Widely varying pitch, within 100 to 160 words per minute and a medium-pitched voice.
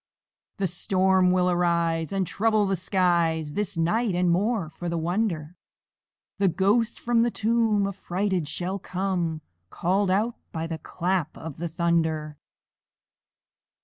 No: average, 3.1 semitones; slow, 135 wpm; medium, 180 Hz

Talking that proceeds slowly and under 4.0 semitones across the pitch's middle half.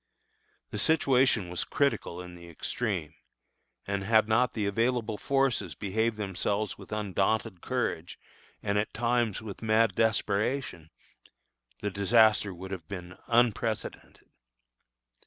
Yes: slow, 120 wpm; average, 3.1 semitones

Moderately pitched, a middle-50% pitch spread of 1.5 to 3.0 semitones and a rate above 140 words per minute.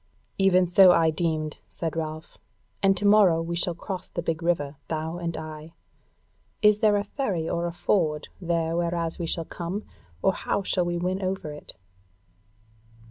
Yes: medium, 170 Hz; narrow, 2.4 semitones; average, 170 wpm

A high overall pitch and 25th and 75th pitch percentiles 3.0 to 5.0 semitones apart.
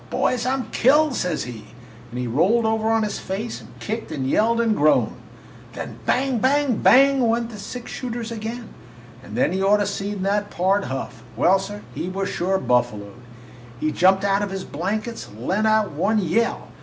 Yes: high, 205 Hz; average, 4.3 semitones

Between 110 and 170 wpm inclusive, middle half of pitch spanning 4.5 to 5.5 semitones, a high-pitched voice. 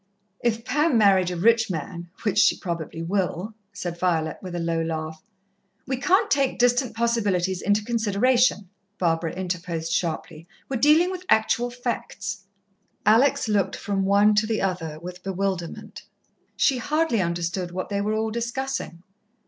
Yes: average, 150 wpm; average, 5.2 semitones; high, 200 Hz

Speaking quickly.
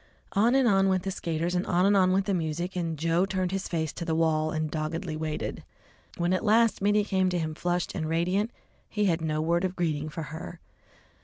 Yes: fast, 225 wpm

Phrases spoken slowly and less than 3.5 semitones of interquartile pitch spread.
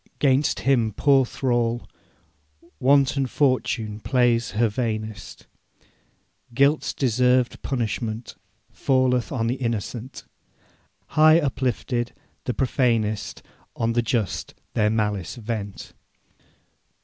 Yes: slow, 90 wpm; average, 3.0 semitones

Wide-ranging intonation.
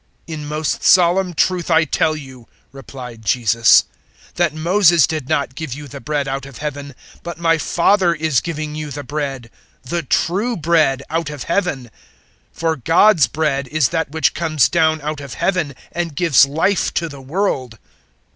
No: average, 3.5 semitones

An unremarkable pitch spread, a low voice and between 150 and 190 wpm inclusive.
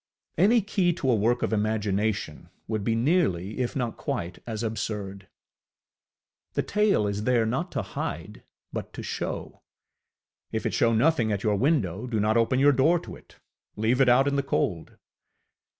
Yes: average, 4.6 semitones; low, 115 Hz; average, 170 wpm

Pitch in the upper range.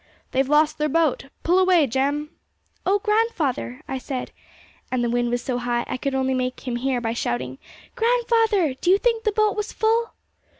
Yes: very high, 285 Hz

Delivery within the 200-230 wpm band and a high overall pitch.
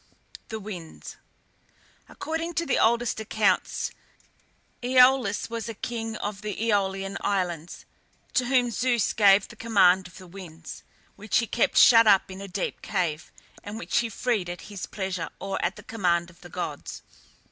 No: average, 160 wpm; high, 205 Hz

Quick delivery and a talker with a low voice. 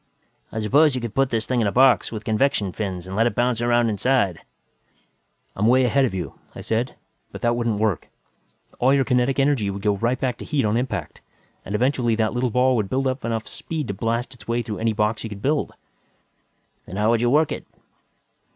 Yes: fast, 225 wpm; low, 115 Hz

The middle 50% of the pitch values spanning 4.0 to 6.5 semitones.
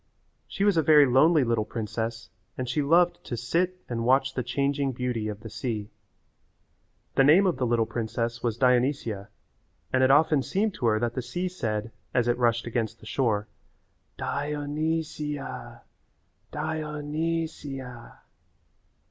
Yes: average, 4.5 semitones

